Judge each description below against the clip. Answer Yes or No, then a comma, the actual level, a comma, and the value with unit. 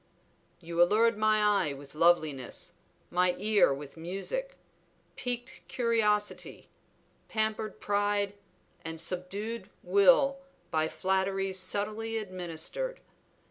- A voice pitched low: No, high, 200 Hz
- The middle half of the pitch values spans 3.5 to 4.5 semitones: Yes, average, 3.8 semitones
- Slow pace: Yes, slow, 95 wpm